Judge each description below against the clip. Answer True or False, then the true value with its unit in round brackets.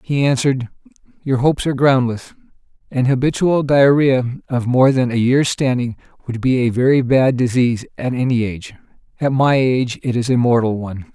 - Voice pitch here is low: True (125 Hz)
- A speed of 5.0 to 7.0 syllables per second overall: True (5.5 syllables/s)